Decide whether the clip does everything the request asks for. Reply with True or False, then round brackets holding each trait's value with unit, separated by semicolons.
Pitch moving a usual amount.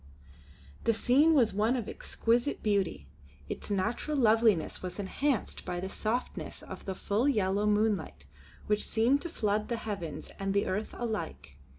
True (3.4 semitones)